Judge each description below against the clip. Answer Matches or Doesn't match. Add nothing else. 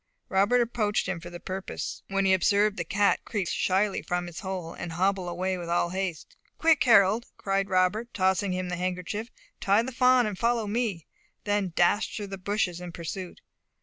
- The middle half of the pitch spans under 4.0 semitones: Matches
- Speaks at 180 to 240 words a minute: Matches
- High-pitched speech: Matches